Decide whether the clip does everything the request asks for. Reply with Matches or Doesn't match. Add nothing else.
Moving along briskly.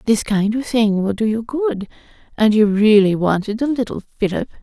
Doesn't match